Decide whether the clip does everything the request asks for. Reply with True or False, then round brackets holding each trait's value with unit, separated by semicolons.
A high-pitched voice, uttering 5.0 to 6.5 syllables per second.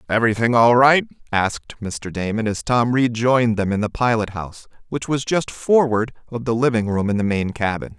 False (115 Hz; 5.4 syllables/s)